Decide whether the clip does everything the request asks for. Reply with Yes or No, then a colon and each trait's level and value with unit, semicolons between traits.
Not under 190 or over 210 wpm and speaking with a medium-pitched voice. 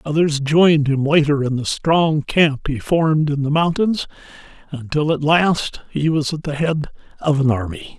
No: average, 180 wpm; medium, 150 Hz